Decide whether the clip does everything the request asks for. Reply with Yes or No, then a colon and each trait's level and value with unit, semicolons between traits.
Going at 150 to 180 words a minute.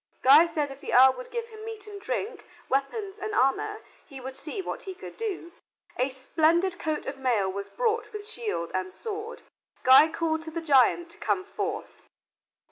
No: average, 190 wpm